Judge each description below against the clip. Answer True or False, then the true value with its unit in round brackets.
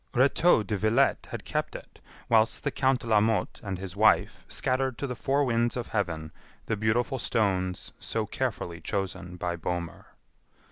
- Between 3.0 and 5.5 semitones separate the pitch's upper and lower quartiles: True (5.1 semitones)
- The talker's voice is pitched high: False (110 Hz)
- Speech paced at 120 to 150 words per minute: False (170 wpm)